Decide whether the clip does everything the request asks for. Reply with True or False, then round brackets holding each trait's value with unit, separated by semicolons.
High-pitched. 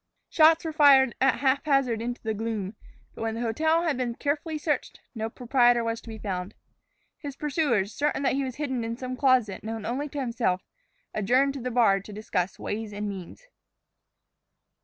True (245 Hz)